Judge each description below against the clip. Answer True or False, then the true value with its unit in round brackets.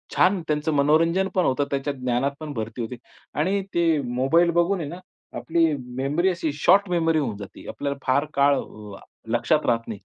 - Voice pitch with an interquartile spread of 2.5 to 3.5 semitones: False (4.6 semitones)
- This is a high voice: False (150 Hz)